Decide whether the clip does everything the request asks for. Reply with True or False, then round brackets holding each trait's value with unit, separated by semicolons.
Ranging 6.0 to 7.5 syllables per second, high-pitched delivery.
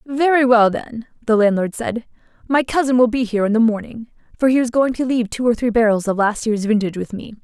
True (6.1 syllables/s; 230 Hz)